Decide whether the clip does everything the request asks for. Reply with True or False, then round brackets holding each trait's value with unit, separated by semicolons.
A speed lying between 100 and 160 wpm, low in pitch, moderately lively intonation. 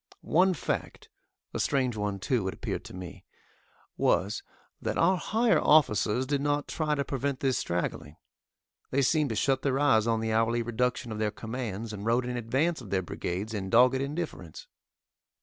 False (175 wpm; 120 Hz; 4.7 semitones)